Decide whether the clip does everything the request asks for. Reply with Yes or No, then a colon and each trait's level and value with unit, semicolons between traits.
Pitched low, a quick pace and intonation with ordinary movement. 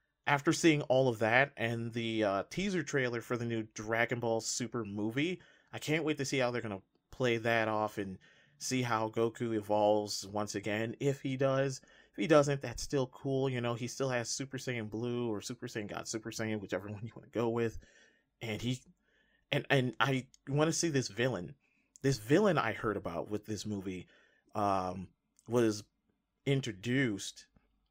No: low, 120 Hz; average, 185 wpm; average, 3.7 semitones